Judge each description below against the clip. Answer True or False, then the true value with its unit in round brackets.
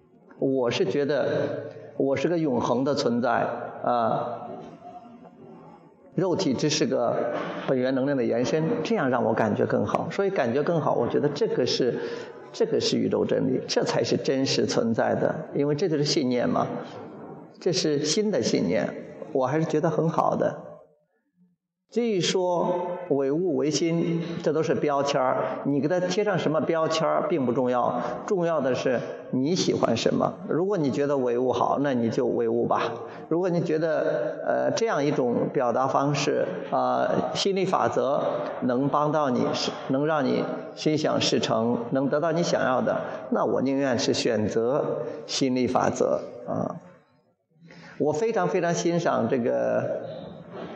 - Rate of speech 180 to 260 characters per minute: True (225 characters per minute)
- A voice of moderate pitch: True (160 Hz)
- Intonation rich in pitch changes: False (4.3 semitones)